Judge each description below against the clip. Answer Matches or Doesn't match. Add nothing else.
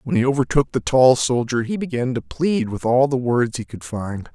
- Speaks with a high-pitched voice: Doesn't match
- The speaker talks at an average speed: Doesn't match